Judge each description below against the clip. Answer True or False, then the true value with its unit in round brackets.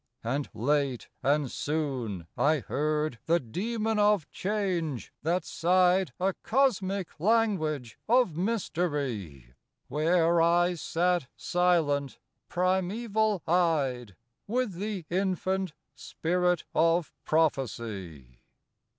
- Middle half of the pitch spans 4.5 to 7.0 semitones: True (5.0 semitones)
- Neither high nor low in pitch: True (170 Hz)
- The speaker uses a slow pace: True (90 wpm)